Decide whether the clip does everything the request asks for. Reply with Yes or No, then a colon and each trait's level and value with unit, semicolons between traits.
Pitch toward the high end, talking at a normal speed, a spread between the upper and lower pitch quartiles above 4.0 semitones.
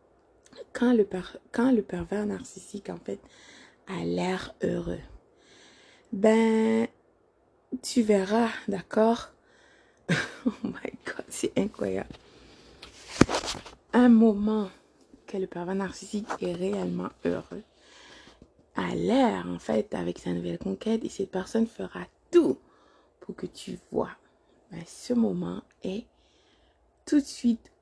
No: high, 215 Hz; slow, 115 wpm; average, 4.4 semitones